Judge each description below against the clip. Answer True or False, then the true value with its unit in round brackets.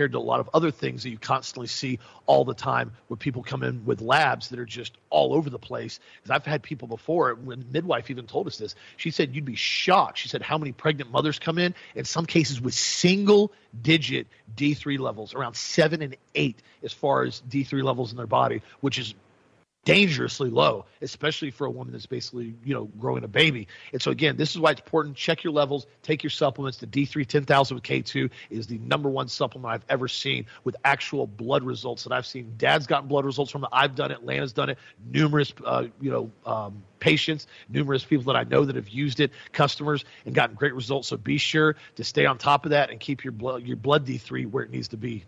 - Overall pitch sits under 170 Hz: True (140 Hz)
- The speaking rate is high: True (230 wpm)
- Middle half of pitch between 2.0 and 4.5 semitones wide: True (3.7 semitones)